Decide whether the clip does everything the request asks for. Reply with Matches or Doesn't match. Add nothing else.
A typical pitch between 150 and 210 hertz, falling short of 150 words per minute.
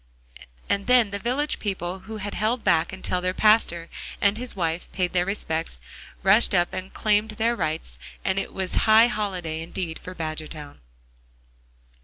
Doesn't match